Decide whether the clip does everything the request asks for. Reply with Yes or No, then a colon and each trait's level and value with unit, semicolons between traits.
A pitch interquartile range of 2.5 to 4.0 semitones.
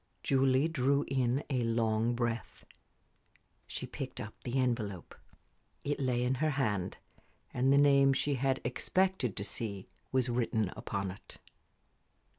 Yes: average, 3.2 semitones